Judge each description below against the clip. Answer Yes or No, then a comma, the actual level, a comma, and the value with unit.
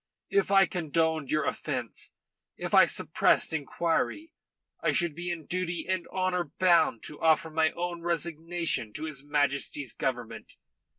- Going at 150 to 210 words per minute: No, average, 140 wpm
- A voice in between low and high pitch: Yes, medium, 165 Hz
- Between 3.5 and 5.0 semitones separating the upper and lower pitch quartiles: No, narrow, 2.5 semitones